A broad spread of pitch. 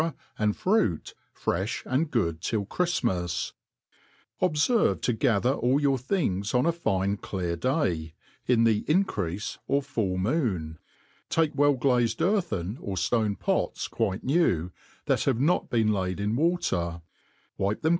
Yes: wide, 7.4 semitones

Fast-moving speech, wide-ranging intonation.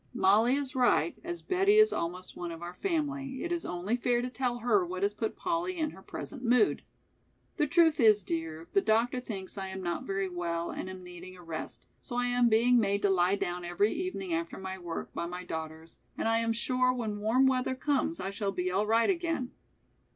Yes: fast, 215 wpm; wide, 5.9 semitones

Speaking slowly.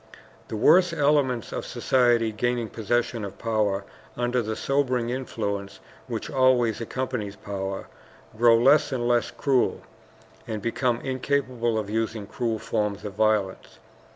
Yes: slow, 130 wpm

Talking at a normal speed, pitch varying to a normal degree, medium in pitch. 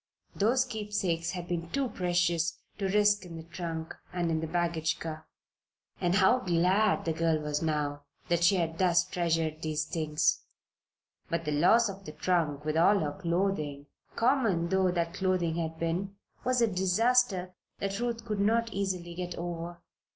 Yes: average, 165 wpm; average, 3.2 semitones; medium, 175 Hz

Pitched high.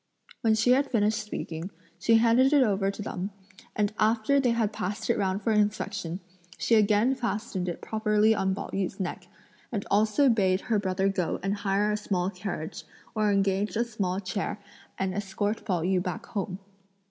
Yes: high, 205 Hz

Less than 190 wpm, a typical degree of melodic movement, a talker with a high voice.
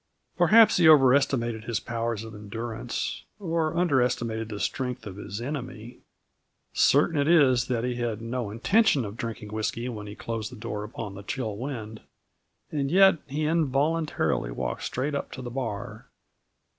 No: average, 165 wpm; average, 4.4 semitones; low, 120 Hz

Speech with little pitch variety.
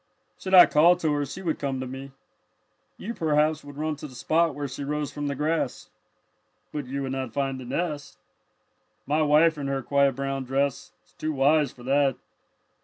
Yes: narrow, 2.2 semitones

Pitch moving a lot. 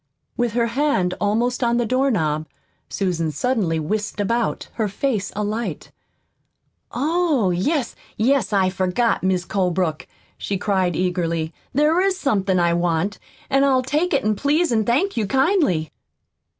Yes: wide, 6.4 semitones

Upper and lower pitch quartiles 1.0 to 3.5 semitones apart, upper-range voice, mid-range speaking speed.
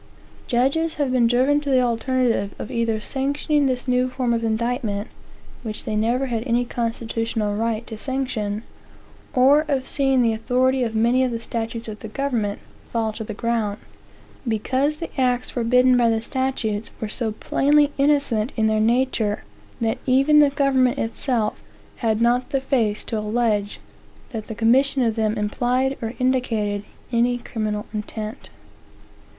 Yes: average, 2.9 semitones; high, 235 Hz; average, 155 wpm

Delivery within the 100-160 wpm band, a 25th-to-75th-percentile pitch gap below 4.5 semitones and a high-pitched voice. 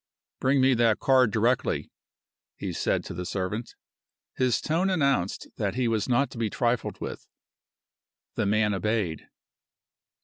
No: average, 140 wpm; average, 3.7 semitones; low, 115 Hz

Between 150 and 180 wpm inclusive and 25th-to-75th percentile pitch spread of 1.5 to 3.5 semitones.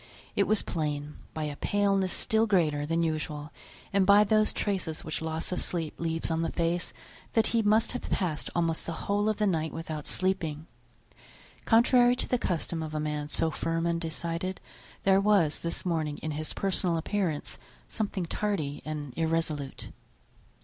No: average, 170 wpm; average, 4.2 semitones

